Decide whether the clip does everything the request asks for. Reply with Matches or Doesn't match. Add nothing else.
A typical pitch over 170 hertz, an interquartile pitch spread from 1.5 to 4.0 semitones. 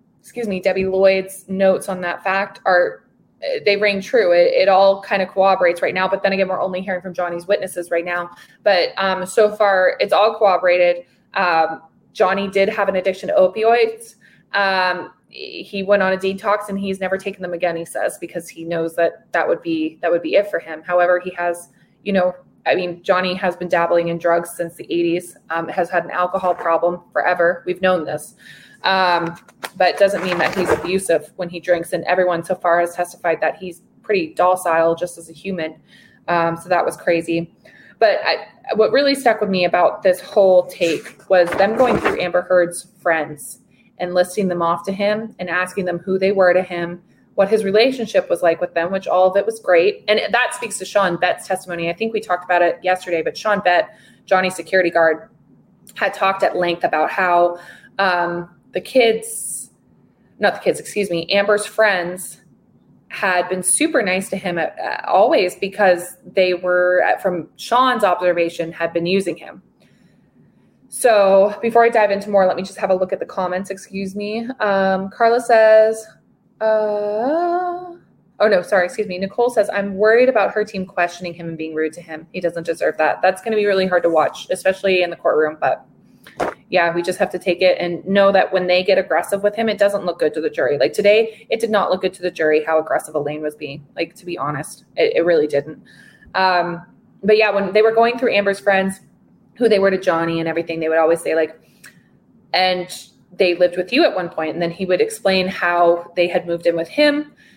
Matches